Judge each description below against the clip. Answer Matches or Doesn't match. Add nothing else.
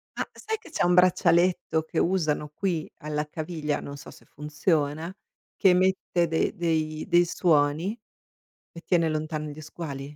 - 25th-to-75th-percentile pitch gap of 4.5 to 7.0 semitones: Doesn't match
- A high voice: Doesn't match